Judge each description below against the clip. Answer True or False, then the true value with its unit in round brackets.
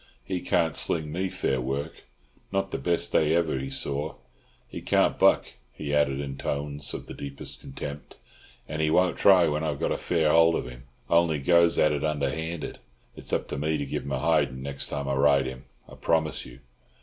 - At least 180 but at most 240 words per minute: True (205 wpm)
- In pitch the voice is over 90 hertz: False (75 Hz)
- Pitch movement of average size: True (3.0 semitones)